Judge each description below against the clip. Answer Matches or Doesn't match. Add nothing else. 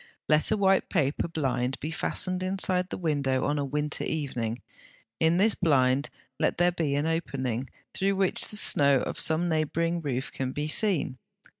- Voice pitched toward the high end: Doesn't match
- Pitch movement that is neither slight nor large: Matches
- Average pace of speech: Matches